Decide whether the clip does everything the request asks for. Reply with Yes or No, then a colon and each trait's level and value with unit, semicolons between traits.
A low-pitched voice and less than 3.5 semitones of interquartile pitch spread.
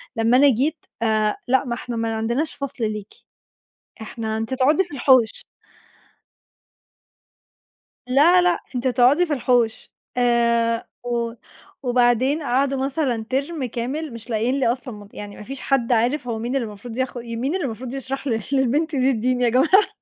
No: very high, 250 Hz; average, 3.0 semitones